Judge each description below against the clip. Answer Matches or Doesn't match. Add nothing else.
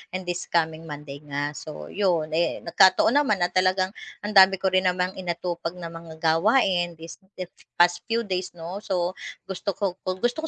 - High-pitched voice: Doesn't match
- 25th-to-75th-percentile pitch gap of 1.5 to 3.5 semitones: Matches